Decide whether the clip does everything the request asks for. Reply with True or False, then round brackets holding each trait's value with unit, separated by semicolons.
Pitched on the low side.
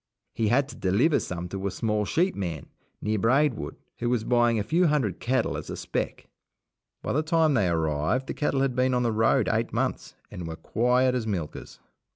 True (115 Hz)